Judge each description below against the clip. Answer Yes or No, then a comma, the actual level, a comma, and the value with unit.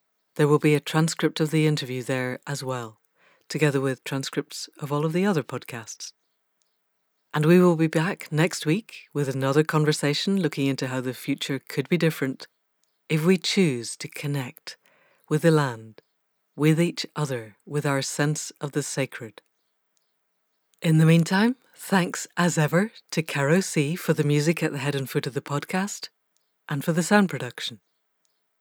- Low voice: No, medium, 150 Hz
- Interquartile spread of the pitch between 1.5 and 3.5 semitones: Yes, average, 3.0 semitones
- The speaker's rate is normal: Yes, average, 170 wpm